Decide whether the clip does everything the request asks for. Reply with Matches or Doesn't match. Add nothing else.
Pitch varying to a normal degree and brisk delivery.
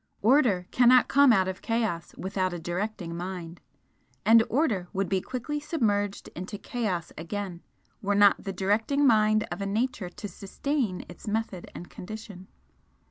Doesn't match